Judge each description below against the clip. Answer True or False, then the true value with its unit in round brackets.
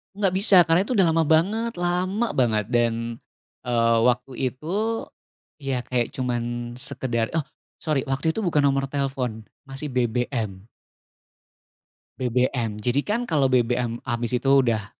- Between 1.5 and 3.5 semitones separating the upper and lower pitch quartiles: False (4.8 semitones)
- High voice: False (130 Hz)